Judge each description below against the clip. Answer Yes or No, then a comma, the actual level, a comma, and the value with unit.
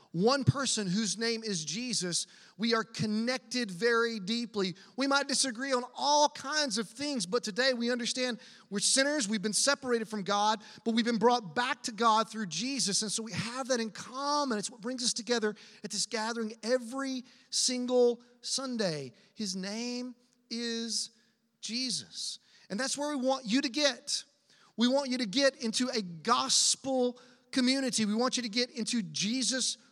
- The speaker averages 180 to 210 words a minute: No, average, 170 wpm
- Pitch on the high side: Yes, high, 235 Hz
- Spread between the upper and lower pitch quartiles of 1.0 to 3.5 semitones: Yes, average, 2.8 semitones